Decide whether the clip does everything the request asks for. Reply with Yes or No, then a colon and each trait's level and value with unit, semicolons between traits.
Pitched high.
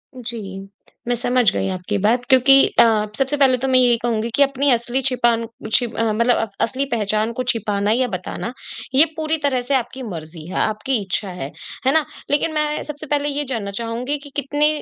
Yes: high, 245 Hz